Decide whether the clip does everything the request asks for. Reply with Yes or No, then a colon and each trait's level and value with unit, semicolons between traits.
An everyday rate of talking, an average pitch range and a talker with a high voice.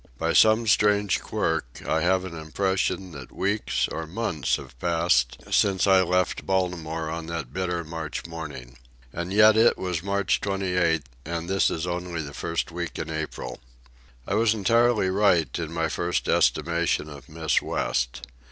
No: average, 160 wpm; average, 3.1 semitones; very low, 85 Hz